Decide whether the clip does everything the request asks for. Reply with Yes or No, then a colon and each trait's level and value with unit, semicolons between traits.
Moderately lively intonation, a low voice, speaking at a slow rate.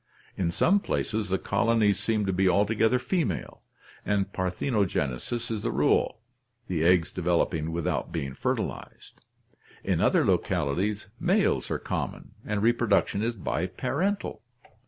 Yes: average, 4.2 semitones; low, 100 Hz; slow, 125 wpm